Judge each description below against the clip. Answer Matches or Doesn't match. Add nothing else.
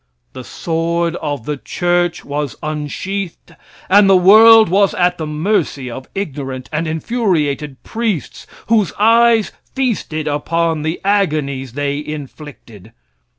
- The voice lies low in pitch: Doesn't match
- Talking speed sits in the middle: Doesn't match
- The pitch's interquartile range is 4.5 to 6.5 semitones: Matches